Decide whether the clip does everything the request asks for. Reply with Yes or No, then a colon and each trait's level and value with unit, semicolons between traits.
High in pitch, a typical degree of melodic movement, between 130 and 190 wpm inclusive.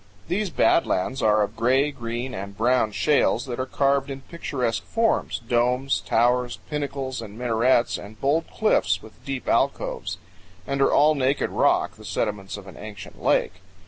No: low, 125 Hz; average, 3.9 semitones; average, 165 wpm